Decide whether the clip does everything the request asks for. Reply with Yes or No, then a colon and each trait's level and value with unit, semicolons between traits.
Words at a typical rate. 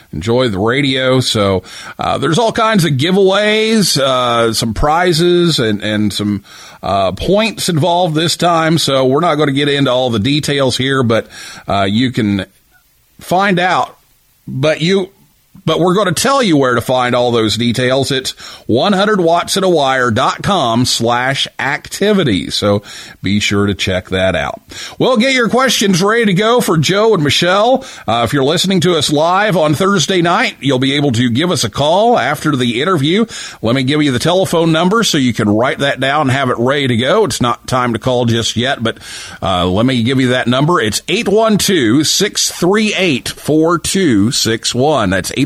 Yes: average, 180 wpm